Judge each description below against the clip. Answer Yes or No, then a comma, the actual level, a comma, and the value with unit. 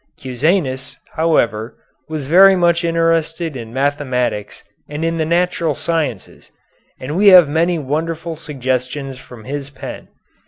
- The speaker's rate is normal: No, slow, 125 wpm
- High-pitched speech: No, medium, 150 Hz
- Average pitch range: Yes, average, 4.1 semitones